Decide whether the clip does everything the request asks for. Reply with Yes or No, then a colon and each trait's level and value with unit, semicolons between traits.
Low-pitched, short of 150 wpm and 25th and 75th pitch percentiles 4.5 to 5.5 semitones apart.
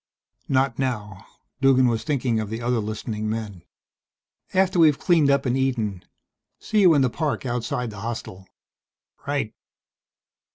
No: low, 125 Hz; average, 140 wpm; average, 4.1 semitones